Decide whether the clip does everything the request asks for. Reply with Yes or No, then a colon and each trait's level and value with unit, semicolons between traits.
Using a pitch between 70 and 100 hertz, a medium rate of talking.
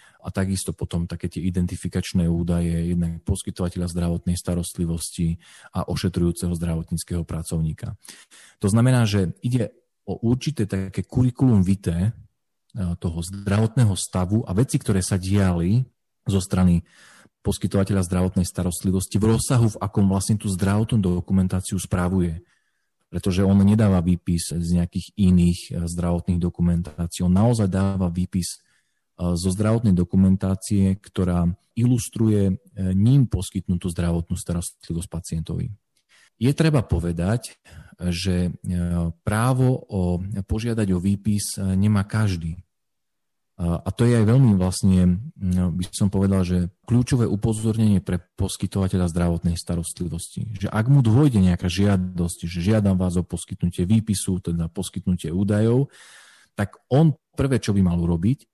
Yes: very low, 95 Hz; average, 120 wpm